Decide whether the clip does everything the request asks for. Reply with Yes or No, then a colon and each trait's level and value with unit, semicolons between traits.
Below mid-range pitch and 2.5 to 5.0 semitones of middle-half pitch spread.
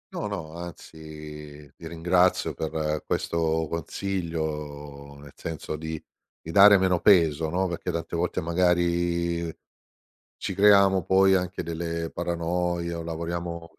No: very low, 85 Hz; narrow, 1.8 semitones